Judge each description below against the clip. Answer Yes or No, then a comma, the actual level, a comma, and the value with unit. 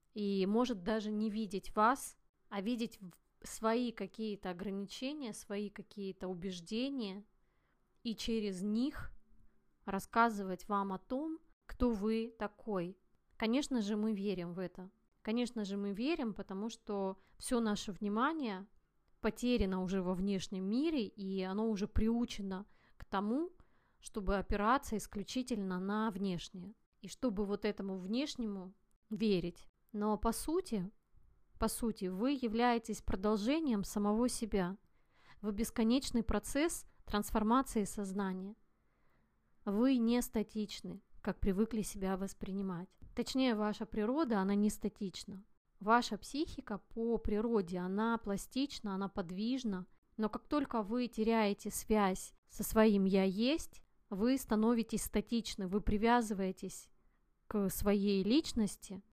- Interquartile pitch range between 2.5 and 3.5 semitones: Yes, average, 2.8 semitones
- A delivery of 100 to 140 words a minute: Yes, average, 115 wpm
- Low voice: No, high, 215 Hz